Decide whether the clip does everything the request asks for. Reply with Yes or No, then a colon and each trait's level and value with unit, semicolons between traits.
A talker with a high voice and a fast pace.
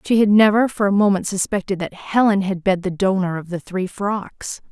Yes: high, 195 Hz; fast, 215 wpm